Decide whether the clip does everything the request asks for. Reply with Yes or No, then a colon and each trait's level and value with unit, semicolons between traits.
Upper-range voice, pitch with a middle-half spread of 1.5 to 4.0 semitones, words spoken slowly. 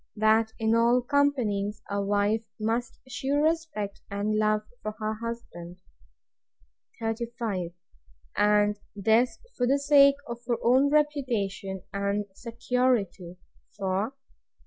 Yes: high, 220 Hz; average, 3.4 semitones; slow, 115 wpm